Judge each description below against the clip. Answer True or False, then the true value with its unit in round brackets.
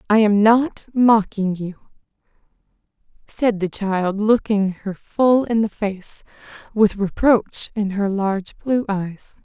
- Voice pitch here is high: True (210 Hz)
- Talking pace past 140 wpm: False (135 wpm)